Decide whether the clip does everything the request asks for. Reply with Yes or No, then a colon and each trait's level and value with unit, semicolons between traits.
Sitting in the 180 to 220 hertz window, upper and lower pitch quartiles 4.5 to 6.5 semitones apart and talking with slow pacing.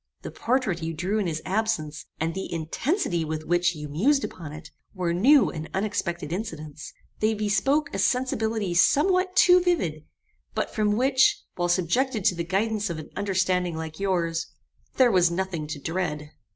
No: medium, 185 Hz; average, 5.3 semitones; average, 165 wpm